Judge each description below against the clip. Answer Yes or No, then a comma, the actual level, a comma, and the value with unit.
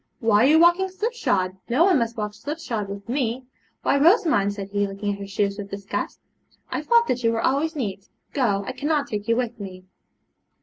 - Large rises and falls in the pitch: Yes, wide, 6.5 semitones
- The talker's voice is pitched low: No, high, 230 Hz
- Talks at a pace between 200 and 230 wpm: Yes, fast, 205 wpm